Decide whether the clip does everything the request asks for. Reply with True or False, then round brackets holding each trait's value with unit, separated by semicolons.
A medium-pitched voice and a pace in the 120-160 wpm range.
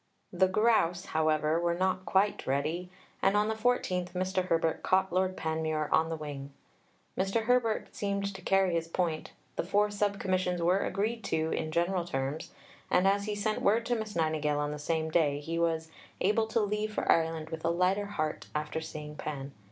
False (180 Hz; 190 wpm)